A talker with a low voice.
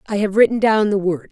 No: high, 205 Hz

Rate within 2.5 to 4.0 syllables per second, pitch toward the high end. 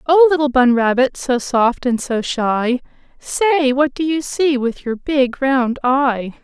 Yes: 3.7 syllables/s; very high, 265 Hz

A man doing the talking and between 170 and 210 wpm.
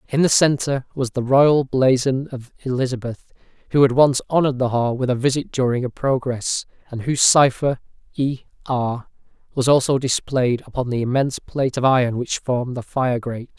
Yes: male; average, 175 wpm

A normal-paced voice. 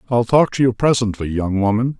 No: fast, 210 wpm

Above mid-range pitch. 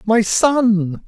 Yes: high, 210 Hz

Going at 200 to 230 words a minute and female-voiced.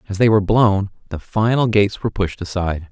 No: fast, 205 wpm; male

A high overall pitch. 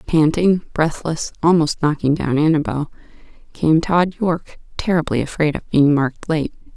No: medium, 155 Hz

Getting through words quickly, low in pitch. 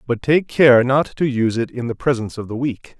Yes: fast, 260 wpm; low, 125 Hz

